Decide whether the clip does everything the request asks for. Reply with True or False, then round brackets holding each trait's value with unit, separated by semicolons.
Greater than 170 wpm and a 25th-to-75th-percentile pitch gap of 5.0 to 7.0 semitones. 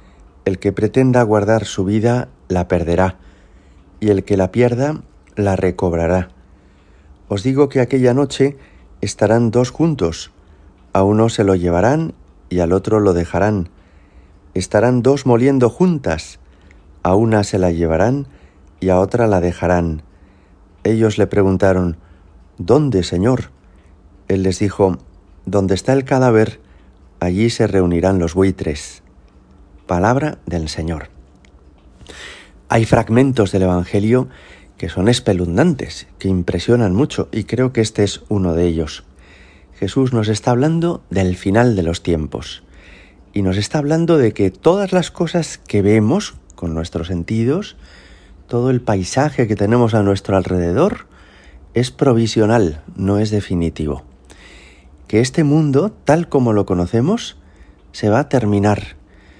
False (135 wpm; 5.6 semitones)